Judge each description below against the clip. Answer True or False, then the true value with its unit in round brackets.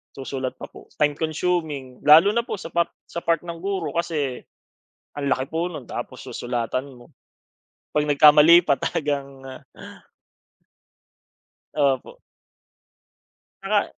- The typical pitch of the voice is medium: True (150 Hz)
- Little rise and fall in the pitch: False (3.8 semitones)